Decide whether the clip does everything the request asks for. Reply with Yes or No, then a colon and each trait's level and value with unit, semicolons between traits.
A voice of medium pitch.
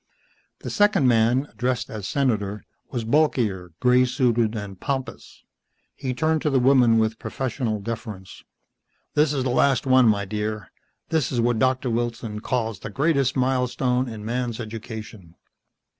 No: low, 120 Hz